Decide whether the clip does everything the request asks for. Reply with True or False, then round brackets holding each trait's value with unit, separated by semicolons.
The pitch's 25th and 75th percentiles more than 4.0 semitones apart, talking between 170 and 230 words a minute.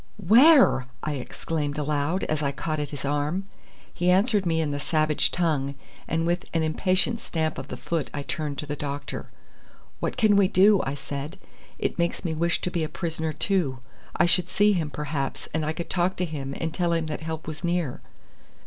False (3.4 semitones; 200 wpm)